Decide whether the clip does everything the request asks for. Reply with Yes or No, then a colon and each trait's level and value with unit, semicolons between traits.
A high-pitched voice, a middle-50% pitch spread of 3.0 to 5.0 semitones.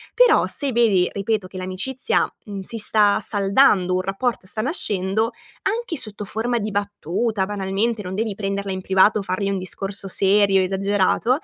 No: high, 200 Hz; narrow, 2.6 semitones